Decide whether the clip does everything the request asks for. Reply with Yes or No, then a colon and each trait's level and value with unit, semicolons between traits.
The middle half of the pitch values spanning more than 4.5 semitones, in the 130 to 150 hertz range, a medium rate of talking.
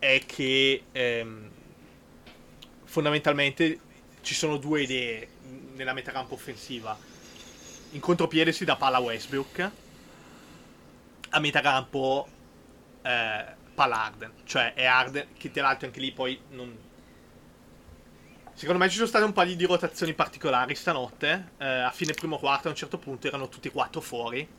No: average, 3.8 semitones; low, 135 Hz; average, 140 wpm